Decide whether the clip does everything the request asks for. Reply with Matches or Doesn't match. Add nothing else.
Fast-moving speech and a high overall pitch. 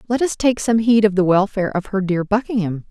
Matches